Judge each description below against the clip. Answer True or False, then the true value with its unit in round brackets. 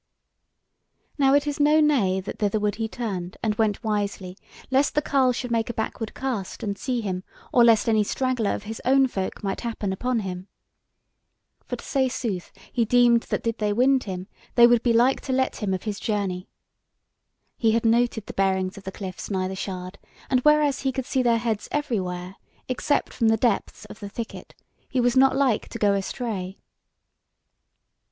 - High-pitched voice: True (225 Hz)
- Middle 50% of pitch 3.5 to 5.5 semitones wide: True (4.2 semitones)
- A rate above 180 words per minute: True (190 wpm)